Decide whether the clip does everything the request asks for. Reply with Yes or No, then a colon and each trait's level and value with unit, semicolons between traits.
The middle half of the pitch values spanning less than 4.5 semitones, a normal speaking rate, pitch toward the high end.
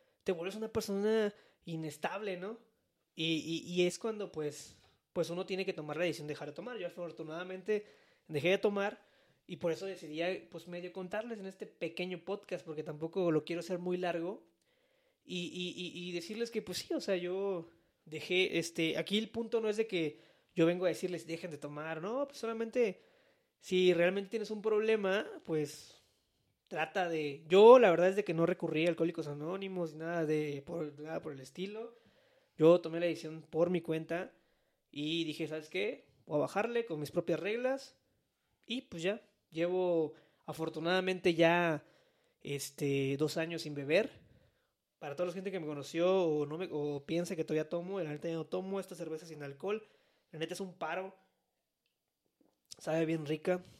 No: average, 3.6 semitones; average, 180 wpm; medium, 175 Hz